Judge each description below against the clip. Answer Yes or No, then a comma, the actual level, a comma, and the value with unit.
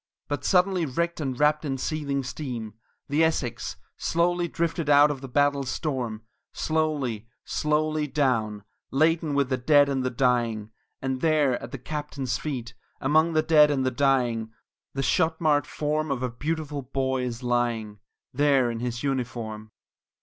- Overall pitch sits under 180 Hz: Yes, medium, 140 Hz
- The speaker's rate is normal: Yes, average, 155 wpm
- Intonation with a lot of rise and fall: No, average, 3.7 semitones